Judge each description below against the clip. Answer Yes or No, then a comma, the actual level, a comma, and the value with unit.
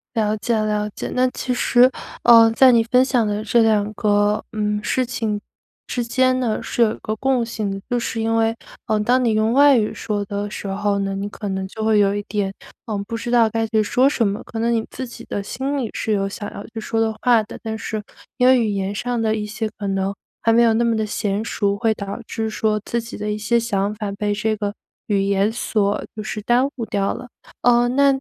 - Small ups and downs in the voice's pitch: Yes, narrow, 2.3 semitones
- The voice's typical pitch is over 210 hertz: Yes, high, 220 Hz